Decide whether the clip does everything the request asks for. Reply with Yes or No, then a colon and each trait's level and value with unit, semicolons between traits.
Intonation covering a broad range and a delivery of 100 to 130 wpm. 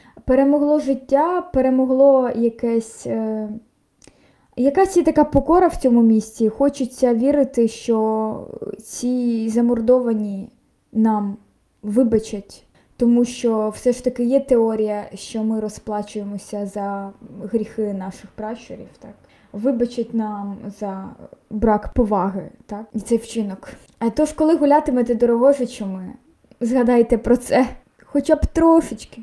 No: average, 3.3 semitones; average, 115 wpm